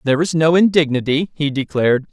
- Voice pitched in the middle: Yes, medium, 150 Hz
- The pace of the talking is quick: No, average, 170 wpm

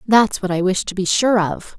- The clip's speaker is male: No, female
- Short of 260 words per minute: No, fast, 270 wpm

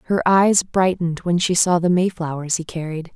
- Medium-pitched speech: Yes, medium, 175 Hz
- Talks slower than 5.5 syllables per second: Yes, 5.1 syllables/s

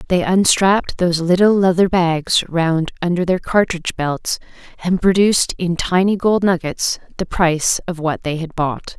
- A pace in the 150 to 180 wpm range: Yes, average, 160 wpm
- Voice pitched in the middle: Yes, medium, 175 Hz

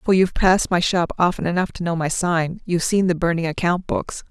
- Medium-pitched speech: Yes, medium, 175 Hz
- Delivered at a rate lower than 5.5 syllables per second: No, 5.9 syllables/s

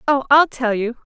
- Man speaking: No, female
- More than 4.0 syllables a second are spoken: Yes, 4.7 syllables/s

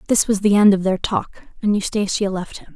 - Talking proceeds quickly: Yes, fast, 240 wpm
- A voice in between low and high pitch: No, high, 200 Hz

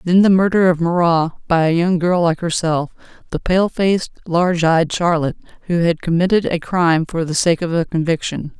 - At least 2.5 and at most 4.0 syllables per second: No, 5.4 syllables/s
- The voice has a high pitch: No, medium, 170 Hz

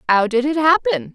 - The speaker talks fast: Yes, fast, 210 wpm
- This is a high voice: Yes, very high, 260 Hz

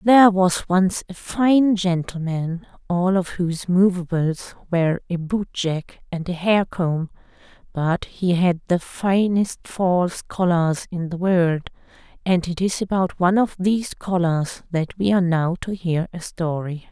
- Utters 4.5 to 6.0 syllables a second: No, 4.1 syllables/s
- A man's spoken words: No, female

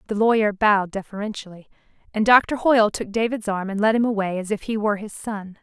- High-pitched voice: Yes, high, 210 Hz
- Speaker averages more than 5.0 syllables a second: Yes, 6.3 syllables/s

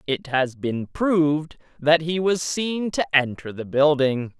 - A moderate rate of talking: Yes, average, 165 wpm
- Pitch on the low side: No, medium, 150 Hz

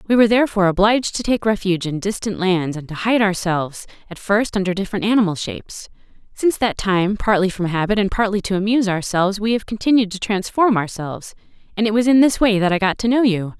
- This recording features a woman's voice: Yes, female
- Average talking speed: No, fast, 215 wpm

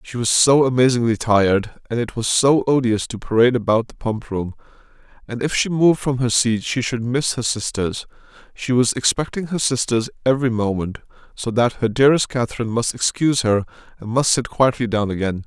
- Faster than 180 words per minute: Yes, average, 190 wpm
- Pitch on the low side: Yes, low, 120 Hz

